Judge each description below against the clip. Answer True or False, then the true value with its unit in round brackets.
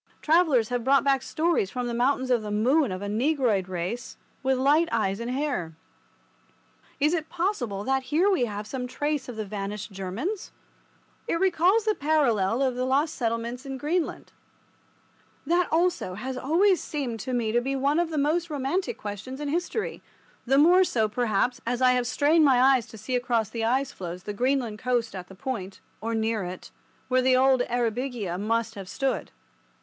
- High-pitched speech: True (255 Hz)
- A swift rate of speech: False (185 wpm)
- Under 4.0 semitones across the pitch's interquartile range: False (4.8 semitones)